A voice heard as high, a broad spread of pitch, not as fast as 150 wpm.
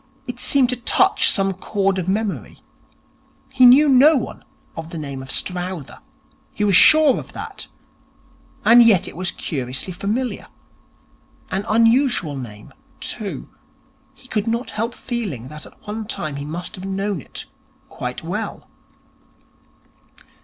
Yes: high, 200 Hz; wide, 6.4 semitones; average, 140 wpm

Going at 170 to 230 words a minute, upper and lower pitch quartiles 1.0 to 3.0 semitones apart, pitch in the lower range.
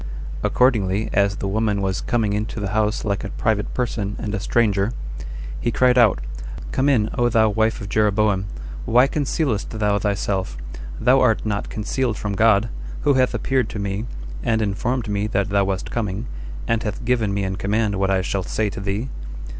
Yes: average, 185 wpm; average, 2.7 semitones; low, 105 Hz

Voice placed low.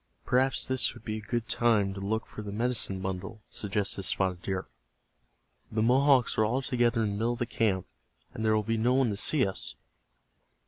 Yes: low, 110 Hz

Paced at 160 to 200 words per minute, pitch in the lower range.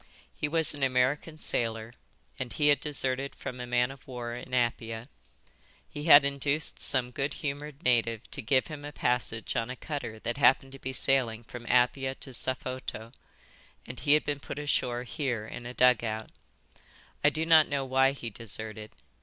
Yes: average, 180 wpm; low, 130 Hz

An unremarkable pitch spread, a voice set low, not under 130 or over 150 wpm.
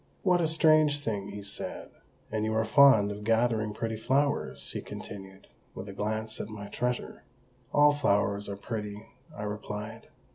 No: average, 3.3 semitones; low, 110 Hz; average, 160 wpm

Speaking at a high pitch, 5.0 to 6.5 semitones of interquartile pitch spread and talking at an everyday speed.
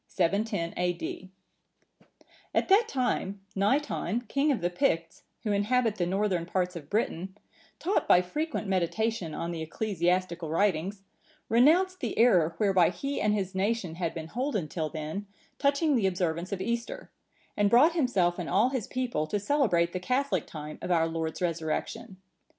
Yes: high, 195 Hz; wide, 5.5 semitones; average, 155 wpm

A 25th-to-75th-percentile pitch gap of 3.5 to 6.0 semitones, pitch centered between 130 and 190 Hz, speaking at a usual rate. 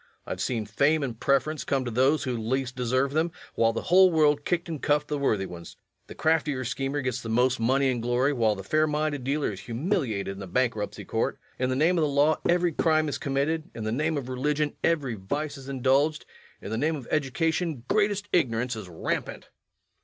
No: average, 4.3 semitones; low, 135 Hz; fast, 215 wpm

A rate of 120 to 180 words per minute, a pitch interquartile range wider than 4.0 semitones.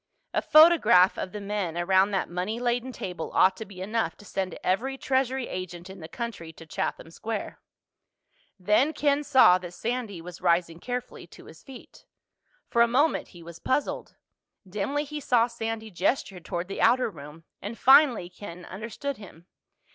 Yes: average, 170 wpm; wide, 5.6 semitones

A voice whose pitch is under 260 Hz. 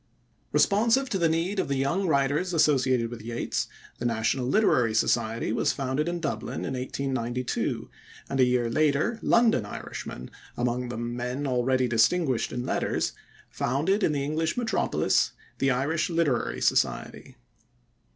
Yes: low, 135 Hz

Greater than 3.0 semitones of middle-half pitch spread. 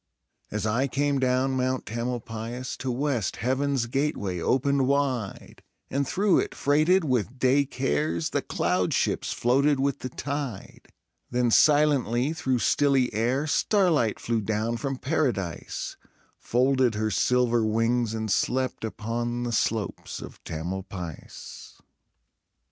Yes: average, 3.8 semitones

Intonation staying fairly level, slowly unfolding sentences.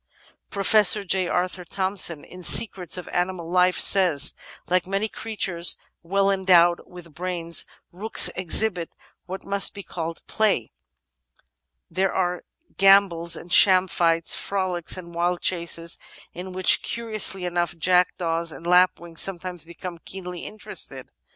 Yes: narrow, 2.0 semitones; slow, 130 wpm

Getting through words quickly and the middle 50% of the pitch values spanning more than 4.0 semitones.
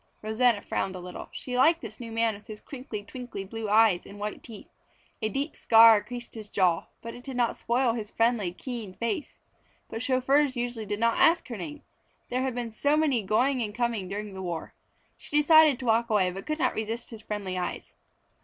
No: fast, 210 wpm; average, 3.3 semitones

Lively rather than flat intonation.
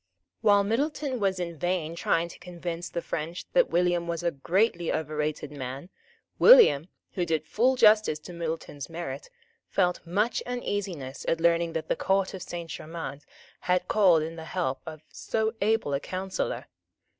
No: average, 3.7 semitones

